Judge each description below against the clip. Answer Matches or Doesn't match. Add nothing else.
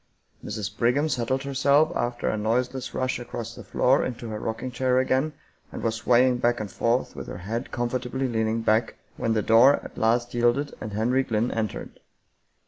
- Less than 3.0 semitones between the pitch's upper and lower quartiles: Matches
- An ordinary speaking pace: Matches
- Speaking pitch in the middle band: Doesn't match